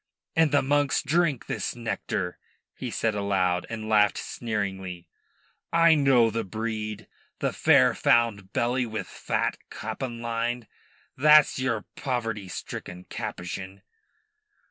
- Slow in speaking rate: Yes, slow, 120 wpm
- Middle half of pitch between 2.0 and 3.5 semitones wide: No, average, 4.2 semitones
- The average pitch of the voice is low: Yes, low, 115 Hz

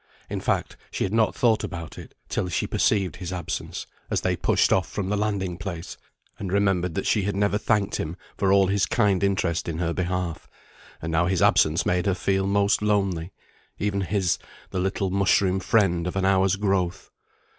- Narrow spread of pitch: Yes, narrow, 2.0 semitones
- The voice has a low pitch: Yes, very low, 95 Hz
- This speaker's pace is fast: No, average, 190 wpm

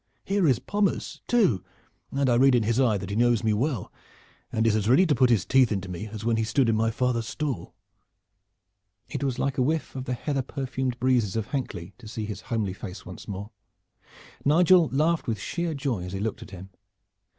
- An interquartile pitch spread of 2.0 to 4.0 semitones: No, average, 4.4 semitones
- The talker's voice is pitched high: No, low, 120 Hz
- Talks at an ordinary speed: No, fast, 215 wpm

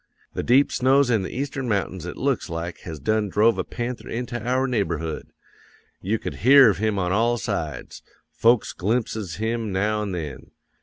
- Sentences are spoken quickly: No, average, 175 wpm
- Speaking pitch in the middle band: No, low, 110 Hz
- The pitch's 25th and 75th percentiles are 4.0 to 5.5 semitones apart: Yes, average, 4.6 semitones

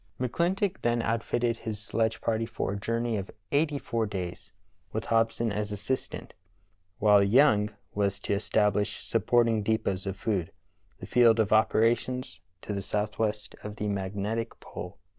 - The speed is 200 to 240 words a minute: No, average, 150 wpm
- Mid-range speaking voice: No, low, 110 Hz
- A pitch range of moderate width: No, narrow, 2.1 semitones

